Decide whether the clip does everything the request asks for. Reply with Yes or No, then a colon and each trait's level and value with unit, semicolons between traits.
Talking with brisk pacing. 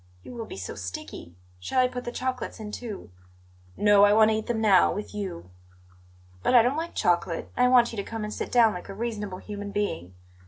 Yes: fast, 230 wpm